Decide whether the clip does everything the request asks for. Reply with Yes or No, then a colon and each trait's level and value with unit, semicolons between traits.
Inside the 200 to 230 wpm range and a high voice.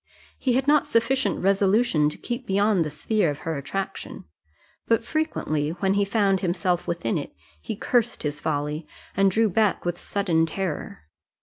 No: average, 165 wpm; high, 195 Hz